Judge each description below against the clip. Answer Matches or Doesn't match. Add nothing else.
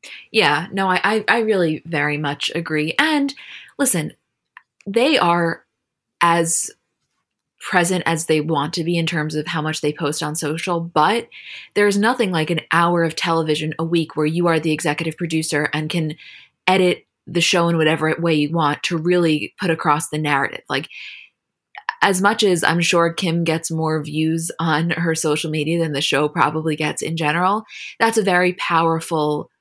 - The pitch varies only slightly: Matches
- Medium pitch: Matches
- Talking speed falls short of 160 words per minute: Doesn't match